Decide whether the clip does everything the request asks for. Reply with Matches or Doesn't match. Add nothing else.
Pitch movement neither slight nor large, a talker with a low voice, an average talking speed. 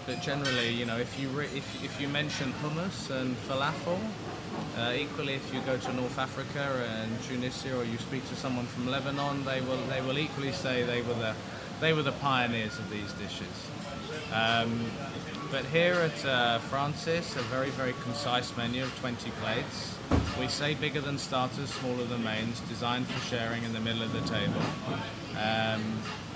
Matches